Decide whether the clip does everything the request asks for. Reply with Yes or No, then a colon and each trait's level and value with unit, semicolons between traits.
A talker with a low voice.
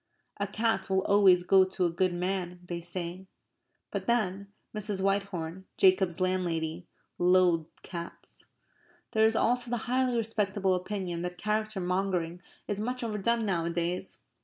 No: high, 190 Hz